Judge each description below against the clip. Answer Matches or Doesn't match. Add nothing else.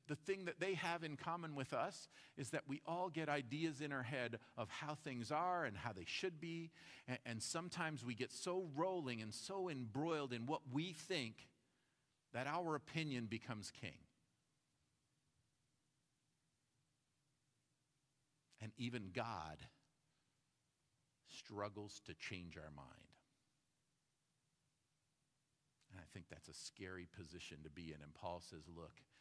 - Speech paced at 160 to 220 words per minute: Doesn't match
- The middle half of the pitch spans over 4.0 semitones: Matches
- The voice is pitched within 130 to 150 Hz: Matches